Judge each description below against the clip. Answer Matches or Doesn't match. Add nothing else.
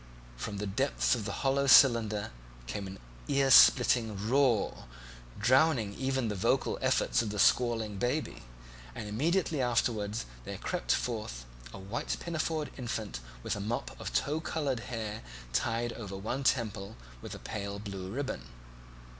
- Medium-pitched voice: Doesn't match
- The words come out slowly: Doesn't match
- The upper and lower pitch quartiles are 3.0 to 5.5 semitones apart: Matches